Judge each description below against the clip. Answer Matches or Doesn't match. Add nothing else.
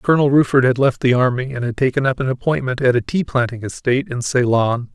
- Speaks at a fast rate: Matches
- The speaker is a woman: Doesn't match